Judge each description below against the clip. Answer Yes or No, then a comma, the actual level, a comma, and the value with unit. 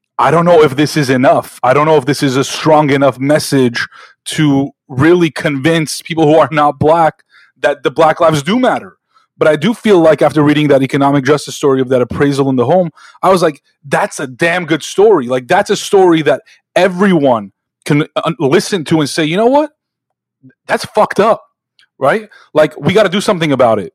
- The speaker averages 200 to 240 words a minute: Yes, fast, 205 wpm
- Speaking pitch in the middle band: Yes, medium, 155 Hz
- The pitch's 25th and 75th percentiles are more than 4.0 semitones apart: Yes, average, 4.4 semitones